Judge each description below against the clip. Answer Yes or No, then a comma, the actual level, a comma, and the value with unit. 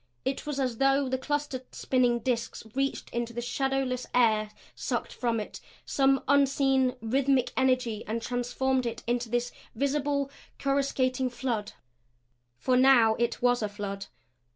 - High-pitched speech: Yes, very high, 255 Hz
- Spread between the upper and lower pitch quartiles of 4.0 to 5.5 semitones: No, narrow, 2.4 semitones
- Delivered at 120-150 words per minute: Yes, average, 140 wpm